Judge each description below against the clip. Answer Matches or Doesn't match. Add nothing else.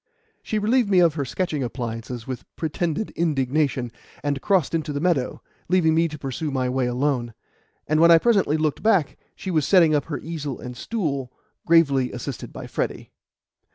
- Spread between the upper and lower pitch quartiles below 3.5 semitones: Doesn't match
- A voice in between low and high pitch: Matches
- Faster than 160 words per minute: Matches